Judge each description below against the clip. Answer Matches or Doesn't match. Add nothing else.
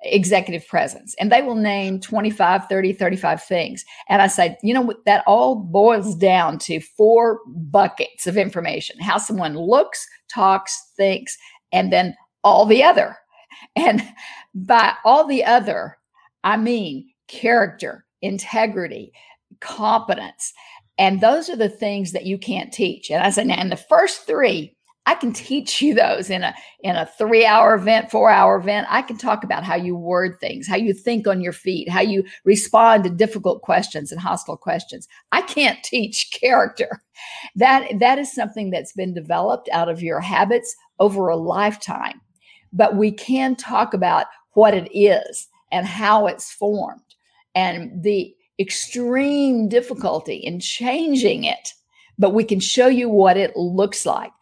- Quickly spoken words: Doesn't match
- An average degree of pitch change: Matches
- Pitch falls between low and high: Doesn't match